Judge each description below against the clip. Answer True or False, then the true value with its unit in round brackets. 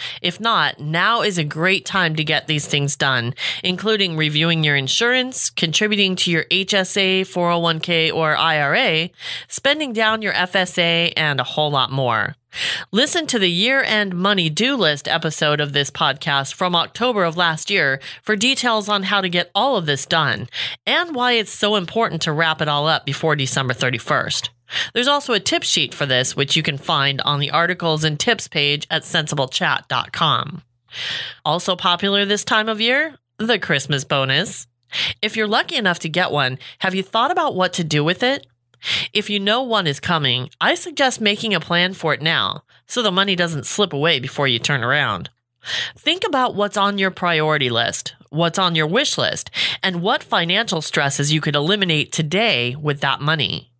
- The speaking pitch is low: False (170 Hz)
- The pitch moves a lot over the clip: True (5.9 semitones)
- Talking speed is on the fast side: False (180 wpm)